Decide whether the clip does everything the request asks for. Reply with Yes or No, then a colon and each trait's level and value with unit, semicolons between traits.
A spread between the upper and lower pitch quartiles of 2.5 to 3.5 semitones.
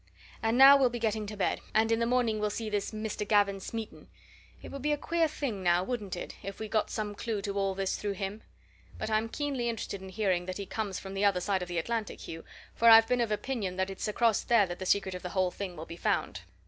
Yes: average, 3.0 semitones